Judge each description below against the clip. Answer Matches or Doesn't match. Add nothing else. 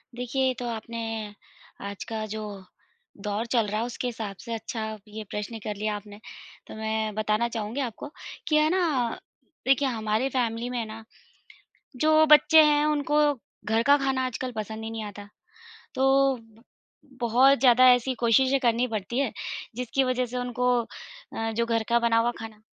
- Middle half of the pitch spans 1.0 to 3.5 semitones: Matches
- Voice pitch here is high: Matches